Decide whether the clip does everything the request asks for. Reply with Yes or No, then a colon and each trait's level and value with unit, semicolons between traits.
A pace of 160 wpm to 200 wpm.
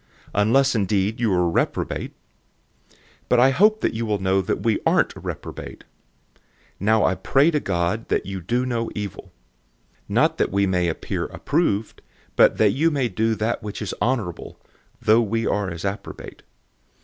Yes: average, 170 wpm